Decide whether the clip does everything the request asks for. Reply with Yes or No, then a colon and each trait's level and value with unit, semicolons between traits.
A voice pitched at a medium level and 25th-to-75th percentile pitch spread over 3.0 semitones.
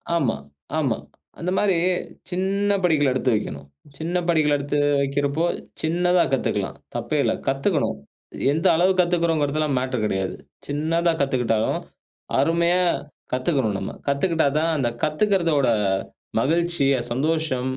Yes: medium, 155 Hz; average, 4.2 semitones